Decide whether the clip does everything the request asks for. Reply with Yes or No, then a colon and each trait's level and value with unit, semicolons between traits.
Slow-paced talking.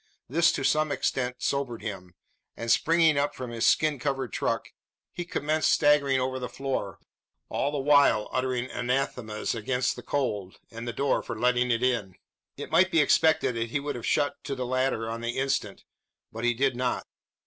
No: average, 185 wpm